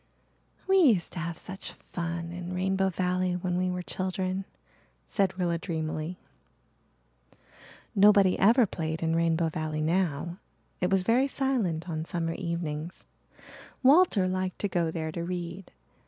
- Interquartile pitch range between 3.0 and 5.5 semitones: No, narrow, 2.4 semitones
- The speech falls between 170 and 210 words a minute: No, average, 140 wpm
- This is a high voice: No, medium, 180 Hz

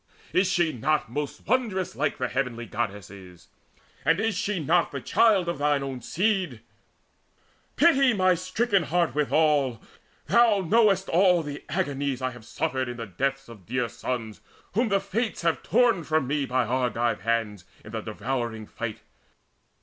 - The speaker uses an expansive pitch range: Yes, wide, 7.8 semitones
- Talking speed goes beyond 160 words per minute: No, average, 155 wpm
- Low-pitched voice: No, medium, 145 Hz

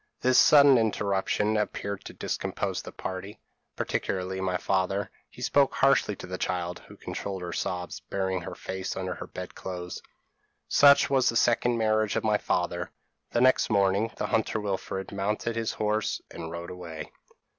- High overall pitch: No, low, 100 Hz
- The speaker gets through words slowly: No, average, 165 wpm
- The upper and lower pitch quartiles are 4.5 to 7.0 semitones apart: No, average, 3.3 semitones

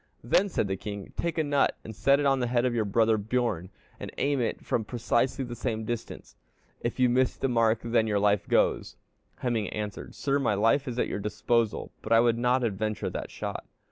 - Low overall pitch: Yes, low, 115 Hz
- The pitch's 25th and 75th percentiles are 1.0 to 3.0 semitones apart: Yes, average, 2.7 semitones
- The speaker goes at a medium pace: No, fast, 220 wpm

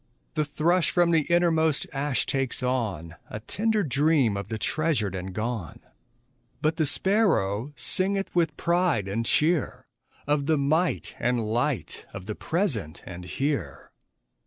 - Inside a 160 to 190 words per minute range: No, average, 140 wpm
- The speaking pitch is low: No, medium, 145 Hz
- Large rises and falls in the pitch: Yes, wide, 6.9 semitones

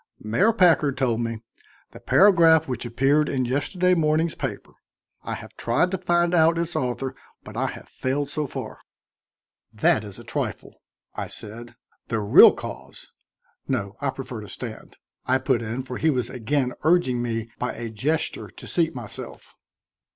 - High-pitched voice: No, low, 130 Hz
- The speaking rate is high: No, average, 165 wpm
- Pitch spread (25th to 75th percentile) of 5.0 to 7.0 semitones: Yes, wide, 5.4 semitones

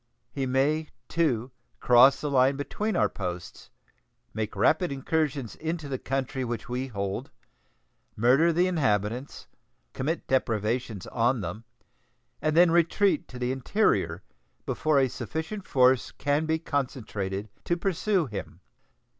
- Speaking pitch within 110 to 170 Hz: Yes, low, 135 Hz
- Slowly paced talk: Yes, slow, 130 wpm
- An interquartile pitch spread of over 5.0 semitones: Yes, wide, 5.4 semitones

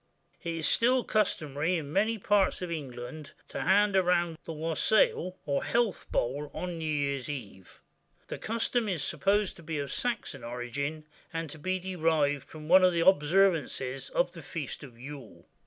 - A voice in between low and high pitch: Yes, medium, 165 Hz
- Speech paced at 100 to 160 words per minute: No, average, 170 wpm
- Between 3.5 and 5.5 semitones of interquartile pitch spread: Yes, average, 4.8 semitones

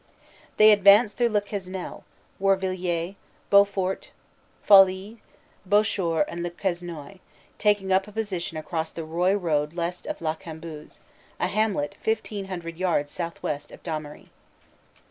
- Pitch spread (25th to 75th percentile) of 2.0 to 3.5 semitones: Yes, average, 3.2 semitones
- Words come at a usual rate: No, slow, 130 wpm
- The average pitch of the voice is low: No, medium, 185 Hz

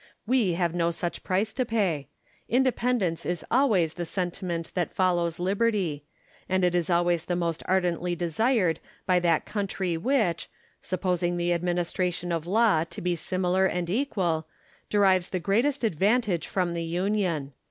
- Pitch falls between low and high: Yes, medium, 180 Hz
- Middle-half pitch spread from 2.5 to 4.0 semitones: Yes, average, 2.8 semitones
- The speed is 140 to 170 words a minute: Yes, average, 150 wpm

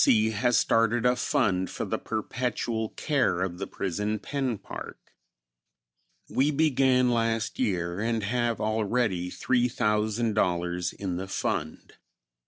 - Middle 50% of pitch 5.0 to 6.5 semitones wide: No, average, 4.2 semitones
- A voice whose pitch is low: Yes, low, 110 Hz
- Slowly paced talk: Yes, slow, 120 wpm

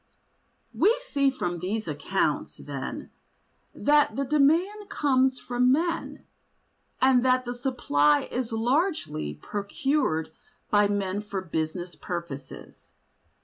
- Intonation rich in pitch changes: Yes, wide, 7.5 semitones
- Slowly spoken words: Yes, slow, 105 wpm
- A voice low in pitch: No, high, 245 Hz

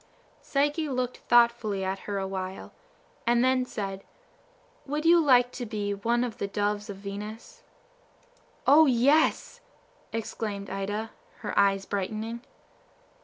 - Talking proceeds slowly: Yes, slow, 125 wpm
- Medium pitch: No, high, 220 Hz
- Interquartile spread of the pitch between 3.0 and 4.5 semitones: Yes, average, 3.9 semitones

